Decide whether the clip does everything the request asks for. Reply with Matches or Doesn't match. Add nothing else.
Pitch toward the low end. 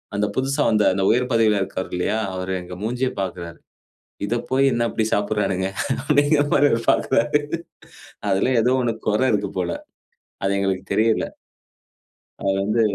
Matches